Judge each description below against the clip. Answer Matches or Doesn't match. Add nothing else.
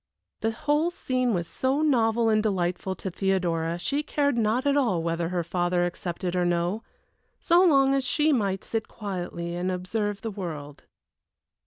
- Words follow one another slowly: Doesn't match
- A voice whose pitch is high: Matches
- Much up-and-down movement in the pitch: Matches